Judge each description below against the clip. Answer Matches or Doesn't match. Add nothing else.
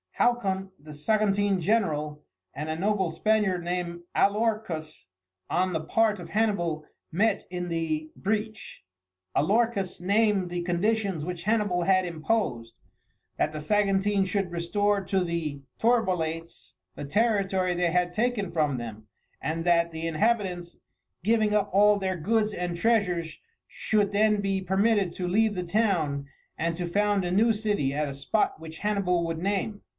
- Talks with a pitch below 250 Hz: Matches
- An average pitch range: Matches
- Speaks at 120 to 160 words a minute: Matches